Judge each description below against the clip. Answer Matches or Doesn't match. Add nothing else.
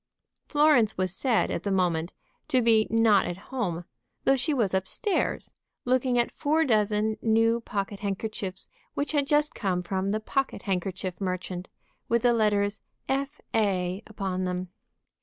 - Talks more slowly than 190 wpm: Matches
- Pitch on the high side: Matches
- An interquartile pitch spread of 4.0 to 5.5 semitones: Matches